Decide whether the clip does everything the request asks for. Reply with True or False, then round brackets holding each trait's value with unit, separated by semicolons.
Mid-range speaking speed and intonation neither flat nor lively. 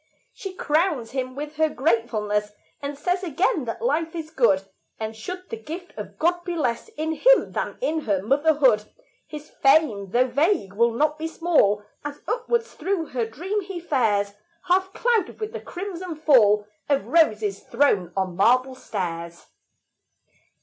False (155 wpm; 7.6 semitones)